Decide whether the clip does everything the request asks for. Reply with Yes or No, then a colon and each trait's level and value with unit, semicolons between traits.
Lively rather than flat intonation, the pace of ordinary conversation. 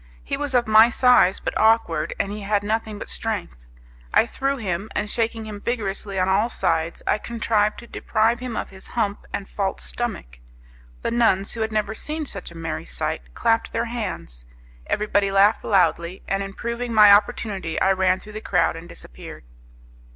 No: average, 3.0 semitones; average, 180 wpm